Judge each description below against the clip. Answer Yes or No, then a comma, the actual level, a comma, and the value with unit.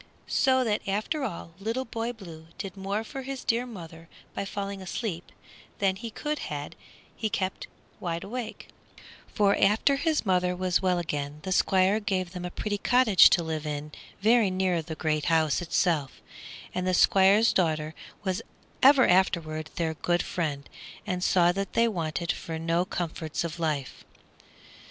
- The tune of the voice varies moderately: Yes, average, 4.3 semitones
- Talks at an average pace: Yes, average, 165 wpm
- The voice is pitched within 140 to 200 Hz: Yes, medium, 185 Hz